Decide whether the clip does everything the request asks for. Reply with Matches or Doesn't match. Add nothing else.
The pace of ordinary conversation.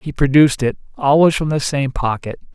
Matches